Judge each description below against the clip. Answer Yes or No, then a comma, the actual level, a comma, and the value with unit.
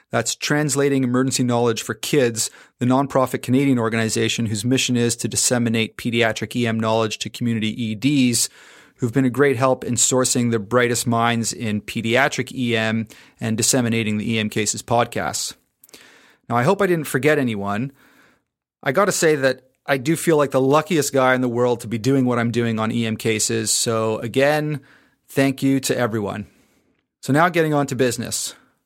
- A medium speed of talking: Yes, average, 175 wpm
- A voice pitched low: Yes, low, 120 Hz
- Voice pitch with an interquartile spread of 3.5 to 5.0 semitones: No, average, 2.9 semitones